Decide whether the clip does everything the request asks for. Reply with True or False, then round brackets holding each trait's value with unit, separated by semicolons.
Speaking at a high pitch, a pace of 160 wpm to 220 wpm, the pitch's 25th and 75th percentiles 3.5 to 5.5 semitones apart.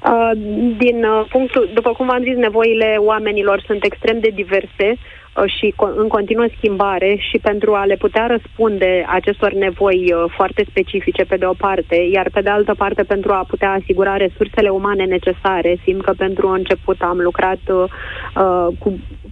False (200 Hz; 170 wpm; 2.4 semitones)